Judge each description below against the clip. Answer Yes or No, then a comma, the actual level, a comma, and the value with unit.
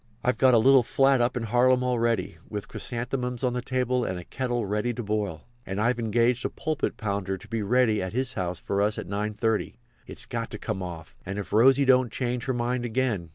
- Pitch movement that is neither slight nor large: Yes, average, 3.3 semitones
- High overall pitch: No, low, 120 Hz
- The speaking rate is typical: No, fast, 225 wpm